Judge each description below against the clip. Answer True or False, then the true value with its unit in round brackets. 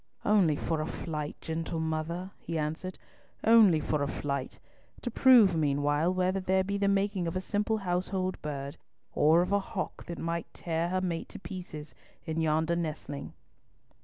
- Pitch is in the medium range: True (170 Hz)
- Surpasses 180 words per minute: False (165 wpm)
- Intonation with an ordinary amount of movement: True (3.4 semitones)